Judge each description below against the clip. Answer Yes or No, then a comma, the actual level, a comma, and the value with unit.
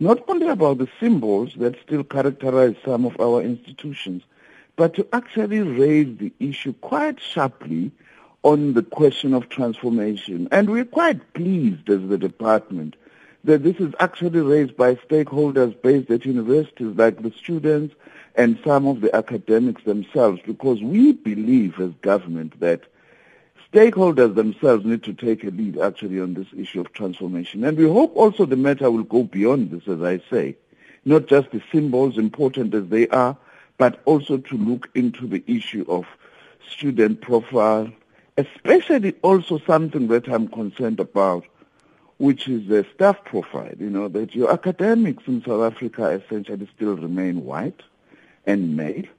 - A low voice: Yes, low, 125 Hz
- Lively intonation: Yes, wide, 6.6 semitones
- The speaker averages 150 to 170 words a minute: Yes, average, 155 wpm